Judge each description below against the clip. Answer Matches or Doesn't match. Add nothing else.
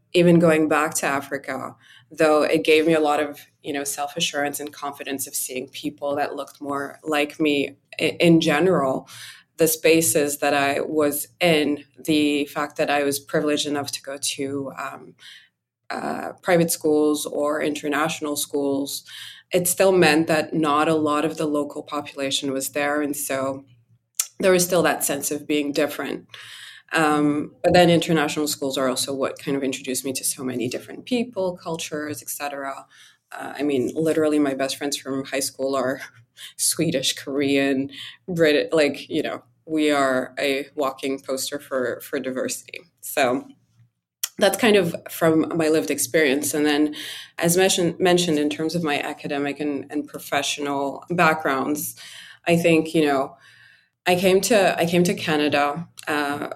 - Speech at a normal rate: Matches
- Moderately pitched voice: Matches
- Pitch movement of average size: Doesn't match